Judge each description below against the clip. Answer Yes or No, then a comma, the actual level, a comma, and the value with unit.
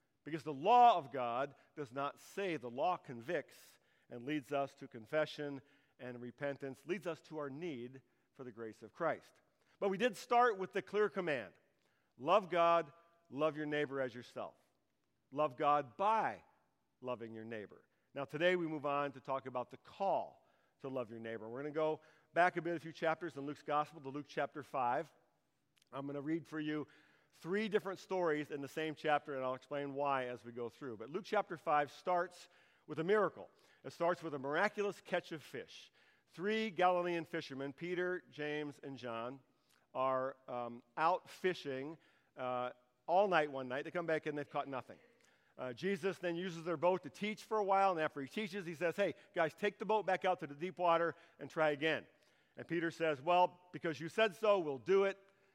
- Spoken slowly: No, average, 195 wpm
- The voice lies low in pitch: No, medium, 155 Hz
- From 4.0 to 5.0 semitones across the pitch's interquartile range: Yes, average, 4.6 semitones